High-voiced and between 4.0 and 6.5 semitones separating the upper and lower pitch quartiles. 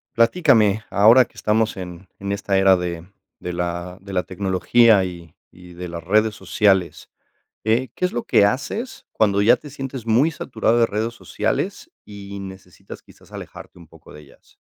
No: low, 100 Hz; average, 4.3 semitones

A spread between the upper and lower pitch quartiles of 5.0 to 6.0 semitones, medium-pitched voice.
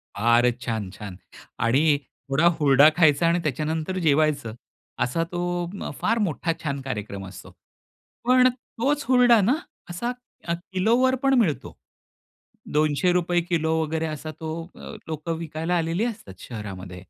Yes: average, 5.3 semitones; medium, 160 Hz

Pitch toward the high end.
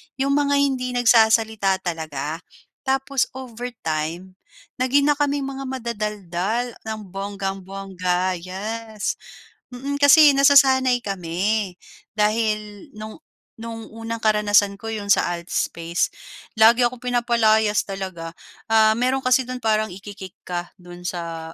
Yes: high, 215 Hz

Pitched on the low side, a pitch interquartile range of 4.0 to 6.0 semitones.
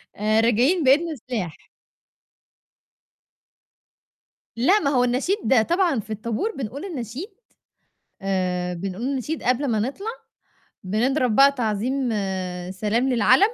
No: very high, 250 Hz; average, 4.6 semitones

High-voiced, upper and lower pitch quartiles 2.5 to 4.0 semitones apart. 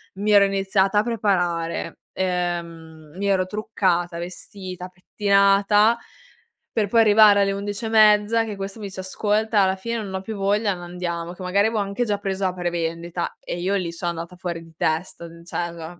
Yes: high, 195 Hz; average, 2.9 semitones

